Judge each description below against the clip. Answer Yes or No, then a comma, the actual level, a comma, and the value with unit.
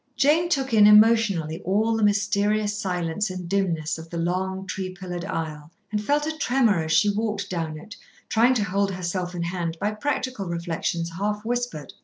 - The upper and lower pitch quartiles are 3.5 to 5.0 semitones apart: Yes, average, 3.9 semitones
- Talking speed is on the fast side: No, average, 180 wpm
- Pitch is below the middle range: No, high, 195 Hz